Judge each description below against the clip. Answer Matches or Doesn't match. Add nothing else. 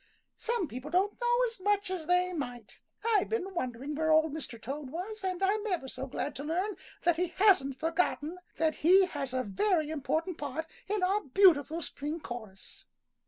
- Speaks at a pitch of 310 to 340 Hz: Matches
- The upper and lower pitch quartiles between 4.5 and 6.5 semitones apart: Matches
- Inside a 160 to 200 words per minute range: Matches